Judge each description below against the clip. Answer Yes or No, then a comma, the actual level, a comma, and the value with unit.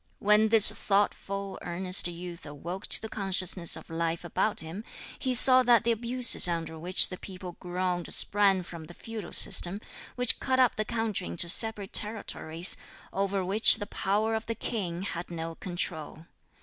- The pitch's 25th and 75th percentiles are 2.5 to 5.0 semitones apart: Yes, average, 3.9 semitones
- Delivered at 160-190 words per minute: Yes, average, 165 wpm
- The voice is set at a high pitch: Yes, high, 195 Hz